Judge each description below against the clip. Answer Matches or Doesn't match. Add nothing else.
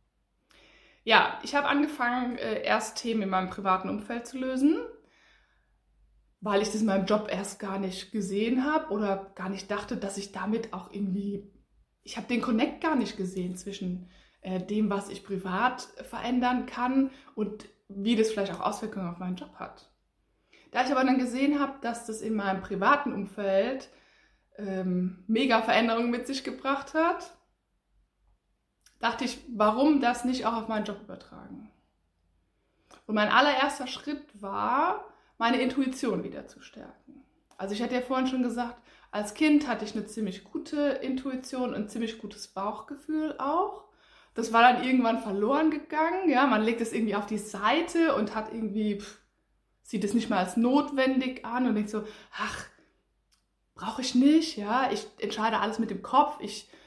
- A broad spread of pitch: Doesn't match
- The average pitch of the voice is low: Doesn't match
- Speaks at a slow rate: Doesn't match